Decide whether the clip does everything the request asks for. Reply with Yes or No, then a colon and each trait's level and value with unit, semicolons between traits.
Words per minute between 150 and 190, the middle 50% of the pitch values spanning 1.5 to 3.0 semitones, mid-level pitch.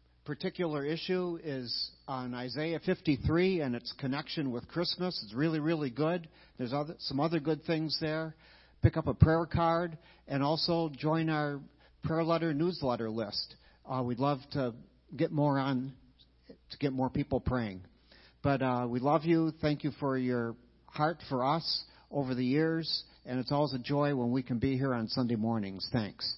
No: average, 175 wpm; average, 4.1 semitones; medium, 145 Hz